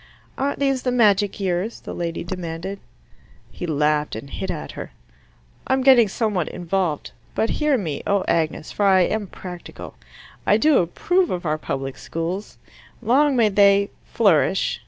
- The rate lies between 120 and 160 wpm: Yes, average, 150 wpm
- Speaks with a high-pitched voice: Yes, high, 195 Hz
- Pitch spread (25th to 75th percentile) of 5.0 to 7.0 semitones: Yes, wide, 5.4 semitones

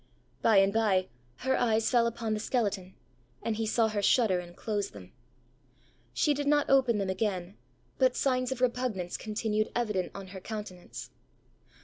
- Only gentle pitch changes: No, average, 3.9 semitones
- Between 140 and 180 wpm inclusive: Yes, average, 160 wpm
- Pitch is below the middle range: No, high, 215 Hz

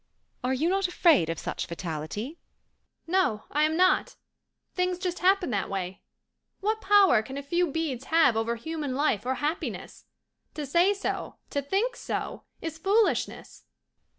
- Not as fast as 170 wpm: Yes, average, 150 wpm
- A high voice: Yes, very high, 310 Hz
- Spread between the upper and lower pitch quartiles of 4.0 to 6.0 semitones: No, wide, 6.6 semitones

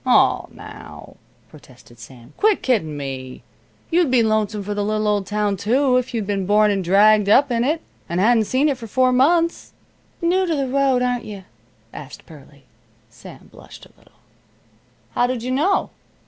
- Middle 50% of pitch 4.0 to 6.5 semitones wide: Yes, average, 4.5 semitones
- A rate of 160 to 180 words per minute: Yes, average, 175 wpm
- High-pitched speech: Yes, high, 220 Hz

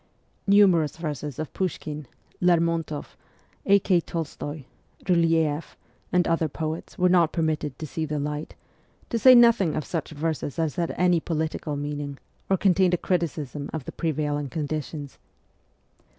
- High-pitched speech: No, medium, 160 Hz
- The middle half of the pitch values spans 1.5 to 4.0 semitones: Yes, average, 2.8 semitones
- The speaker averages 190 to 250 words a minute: No, average, 145 wpm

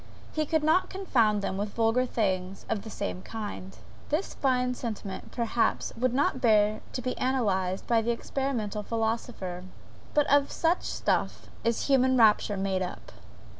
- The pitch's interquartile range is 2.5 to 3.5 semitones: No, average, 4.1 semitones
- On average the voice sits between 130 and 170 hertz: No, high, 230 Hz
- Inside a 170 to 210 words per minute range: No, average, 155 wpm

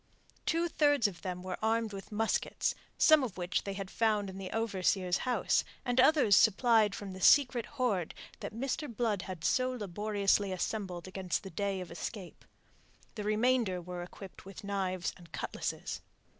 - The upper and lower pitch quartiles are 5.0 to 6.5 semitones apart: No, average, 3.8 semitones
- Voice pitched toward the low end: No, high, 205 Hz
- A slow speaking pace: No, average, 165 wpm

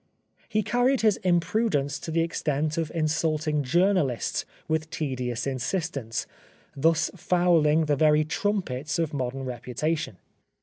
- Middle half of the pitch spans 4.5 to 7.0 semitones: No, average, 3.9 semitones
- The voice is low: No, medium, 155 Hz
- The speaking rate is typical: No, slow, 125 wpm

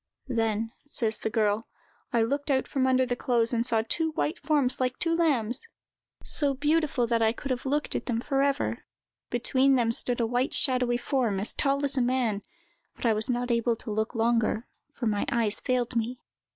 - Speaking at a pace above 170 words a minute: Yes, average, 200 wpm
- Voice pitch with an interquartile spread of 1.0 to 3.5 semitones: Yes, average, 3.1 semitones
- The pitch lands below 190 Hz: No, high, 245 Hz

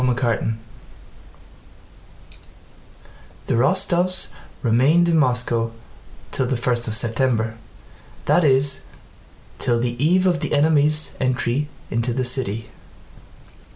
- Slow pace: Yes, slow, 105 wpm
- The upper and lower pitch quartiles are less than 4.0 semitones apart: No, average, 4.3 semitones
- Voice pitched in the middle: No, low, 130 Hz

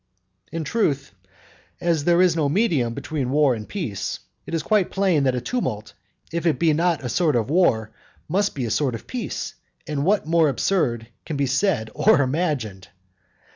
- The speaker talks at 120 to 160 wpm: No, average, 180 wpm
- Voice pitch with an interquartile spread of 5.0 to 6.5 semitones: Yes, wide, 5.6 semitones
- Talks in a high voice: No, medium, 150 Hz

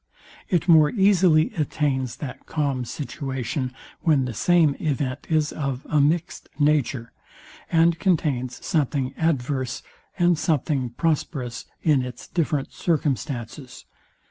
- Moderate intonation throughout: Yes, average, 3.8 semitones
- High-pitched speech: No, medium, 145 Hz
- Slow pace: Yes, slow, 115 wpm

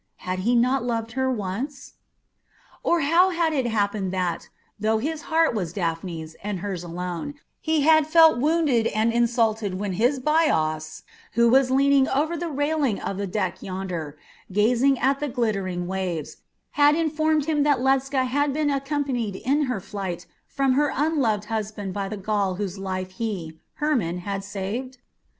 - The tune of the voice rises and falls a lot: Yes, wide, 6.8 semitones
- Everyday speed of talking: Yes, average, 160 wpm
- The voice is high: Yes, high, 235 Hz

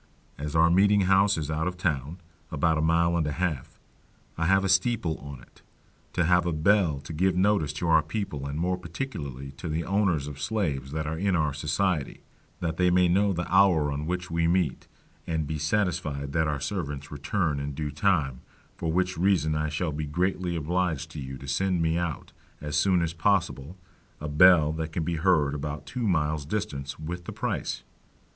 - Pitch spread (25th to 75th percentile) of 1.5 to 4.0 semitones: Yes, average, 3.6 semitones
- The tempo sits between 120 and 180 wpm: No, average, 200 wpm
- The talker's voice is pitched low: Yes, very low, 80 Hz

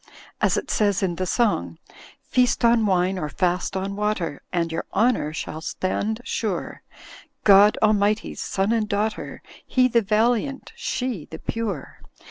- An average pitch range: Yes, average, 3.8 semitones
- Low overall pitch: No, high, 205 Hz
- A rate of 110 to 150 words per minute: Yes, average, 145 wpm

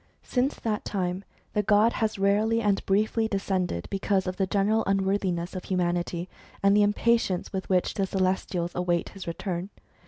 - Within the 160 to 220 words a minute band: Yes, average, 165 wpm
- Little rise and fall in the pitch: Yes, narrow, 2.3 semitones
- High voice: Yes, high, 195 Hz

